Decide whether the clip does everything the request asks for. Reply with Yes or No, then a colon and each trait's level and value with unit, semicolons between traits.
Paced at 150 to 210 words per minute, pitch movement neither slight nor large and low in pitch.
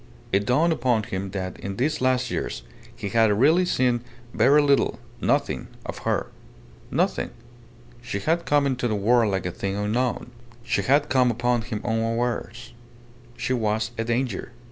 Yes: average, 160 wpm; average, 3.4 semitones; low, 120 Hz